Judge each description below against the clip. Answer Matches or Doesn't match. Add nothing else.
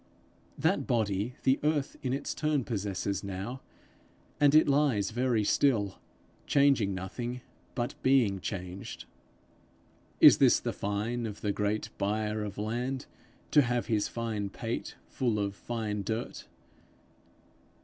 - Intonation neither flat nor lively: Matches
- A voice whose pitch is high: Doesn't match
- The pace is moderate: Doesn't match